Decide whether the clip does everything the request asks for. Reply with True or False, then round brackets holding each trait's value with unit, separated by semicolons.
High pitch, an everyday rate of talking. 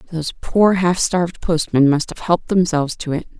False (165 Hz; 195 wpm)